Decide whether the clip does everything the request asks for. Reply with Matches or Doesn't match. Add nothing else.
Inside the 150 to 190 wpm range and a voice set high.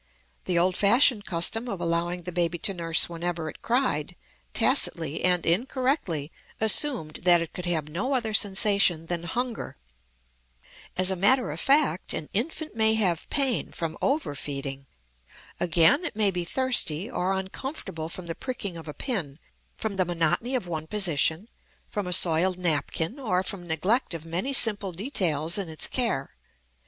Doesn't match